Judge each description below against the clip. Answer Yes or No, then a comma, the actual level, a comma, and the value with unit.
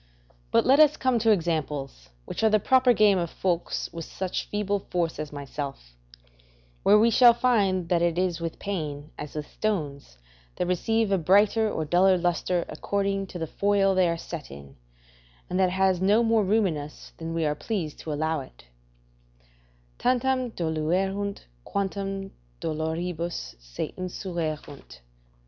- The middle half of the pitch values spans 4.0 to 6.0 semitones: Yes, average, 4.3 semitones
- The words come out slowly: No, average, 165 wpm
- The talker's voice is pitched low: No, medium, 180 Hz